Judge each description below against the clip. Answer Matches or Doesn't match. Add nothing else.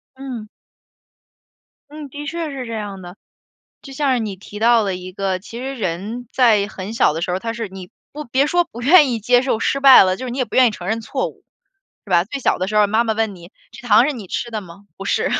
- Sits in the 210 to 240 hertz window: Matches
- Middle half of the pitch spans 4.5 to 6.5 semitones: Matches